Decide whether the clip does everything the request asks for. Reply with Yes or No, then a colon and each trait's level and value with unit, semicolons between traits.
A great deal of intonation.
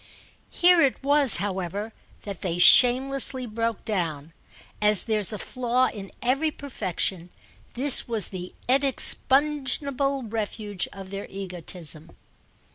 Yes: wide, 5.8 semitones